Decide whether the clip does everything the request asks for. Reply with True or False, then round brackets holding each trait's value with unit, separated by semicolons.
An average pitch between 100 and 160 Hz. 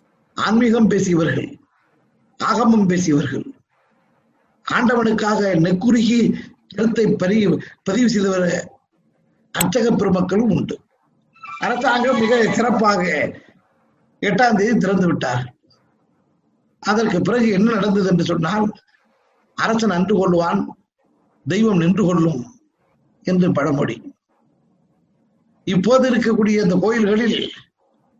False (210 Hz)